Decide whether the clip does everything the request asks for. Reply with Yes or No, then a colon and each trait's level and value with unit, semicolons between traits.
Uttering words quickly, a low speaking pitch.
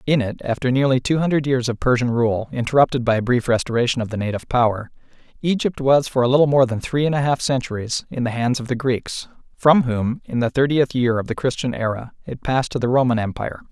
Yes: fast, 225 wpm; low, 125 Hz